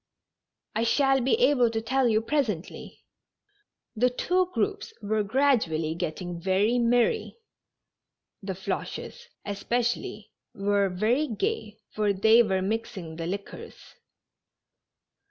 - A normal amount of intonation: Yes, average, 4.5 semitones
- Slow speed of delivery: Yes, slow, 110 wpm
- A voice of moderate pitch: No, high, 220 Hz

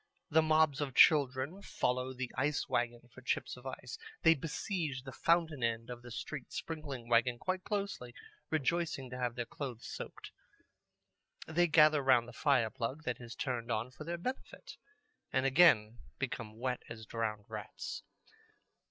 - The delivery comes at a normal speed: Yes, average, 160 wpm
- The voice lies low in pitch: Yes, low, 130 Hz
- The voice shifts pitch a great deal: No, average, 4.5 semitones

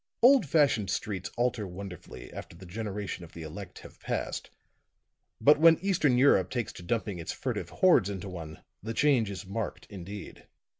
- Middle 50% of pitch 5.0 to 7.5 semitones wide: Yes, wide, 5.6 semitones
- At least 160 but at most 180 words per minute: Yes, average, 165 wpm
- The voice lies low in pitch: Yes, low, 105 Hz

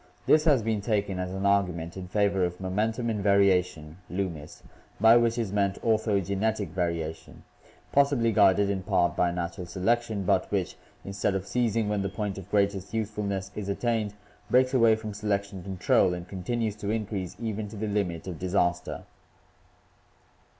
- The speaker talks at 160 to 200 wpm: Yes, average, 165 wpm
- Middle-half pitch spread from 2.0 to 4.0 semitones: Yes, average, 3.0 semitones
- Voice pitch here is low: Yes, low, 100 Hz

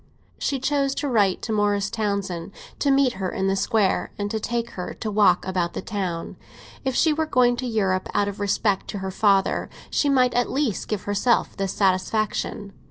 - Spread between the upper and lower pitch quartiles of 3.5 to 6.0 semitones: Yes, average, 4.1 semitones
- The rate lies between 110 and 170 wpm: No, average, 190 wpm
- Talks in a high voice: Yes, high, 205 Hz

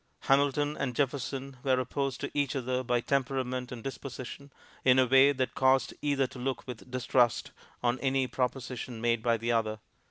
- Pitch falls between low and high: No, low, 130 Hz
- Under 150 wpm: No, average, 170 wpm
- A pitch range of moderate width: No, narrow, 1.7 semitones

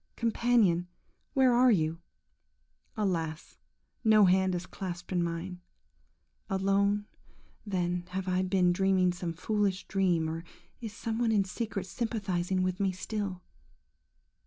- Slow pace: Yes, slow, 125 wpm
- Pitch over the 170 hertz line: Yes, high, 190 Hz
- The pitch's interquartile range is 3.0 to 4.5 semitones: No, narrow, 2.6 semitones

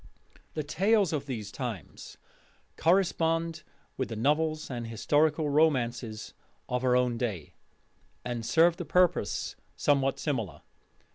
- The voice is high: No, medium, 140 Hz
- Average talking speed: No, slow, 120 wpm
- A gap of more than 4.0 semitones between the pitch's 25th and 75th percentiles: Yes, average, 5.3 semitones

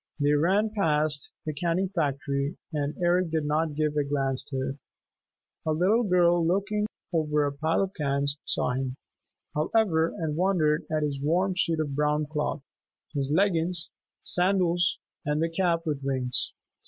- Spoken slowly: No, average, 160 wpm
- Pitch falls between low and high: Yes, medium, 155 Hz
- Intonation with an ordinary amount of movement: Yes, average, 3.4 semitones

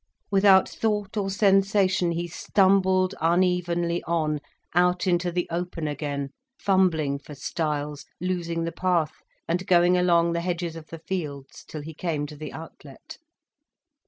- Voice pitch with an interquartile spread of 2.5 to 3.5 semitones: Yes, average, 2.8 semitones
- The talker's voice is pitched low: No, medium, 170 Hz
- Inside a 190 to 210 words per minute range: No, average, 140 wpm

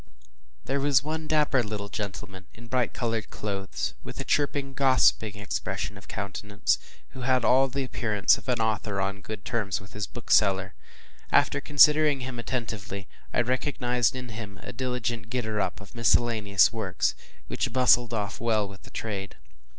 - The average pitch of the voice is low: Yes, low, 115 Hz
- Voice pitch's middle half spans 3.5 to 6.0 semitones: Yes, average, 3.9 semitones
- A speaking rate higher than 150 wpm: Yes, average, 160 wpm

